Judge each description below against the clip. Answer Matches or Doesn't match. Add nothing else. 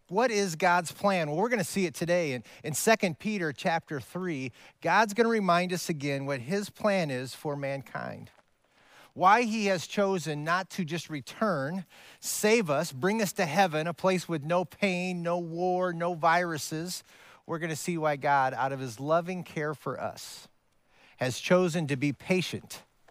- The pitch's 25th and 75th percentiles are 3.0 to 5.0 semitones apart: Matches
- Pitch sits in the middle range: Matches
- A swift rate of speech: Doesn't match